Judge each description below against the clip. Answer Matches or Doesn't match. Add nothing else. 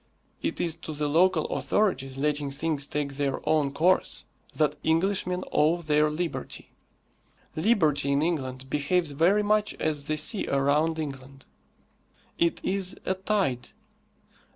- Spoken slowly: Matches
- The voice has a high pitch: Doesn't match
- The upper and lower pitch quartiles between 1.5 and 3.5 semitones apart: Doesn't match